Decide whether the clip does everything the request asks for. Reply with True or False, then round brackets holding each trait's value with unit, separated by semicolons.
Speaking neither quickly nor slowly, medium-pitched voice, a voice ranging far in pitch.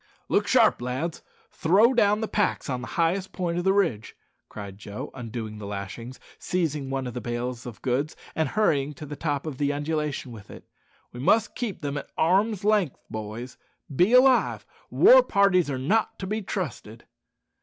True (180 wpm; 150 Hz; 7.7 semitones)